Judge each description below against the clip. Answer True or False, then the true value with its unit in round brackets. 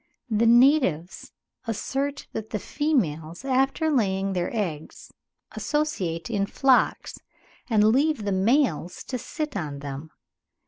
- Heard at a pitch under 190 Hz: False (220 Hz)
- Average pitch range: False (7.3 semitones)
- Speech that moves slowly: True (120 wpm)